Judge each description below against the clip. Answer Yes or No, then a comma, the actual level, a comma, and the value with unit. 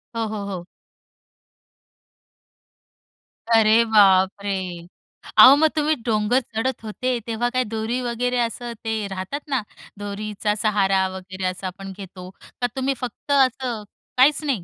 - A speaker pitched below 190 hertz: No, high, 220 Hz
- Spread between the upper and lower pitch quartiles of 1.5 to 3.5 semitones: No, average, 4.0 semitones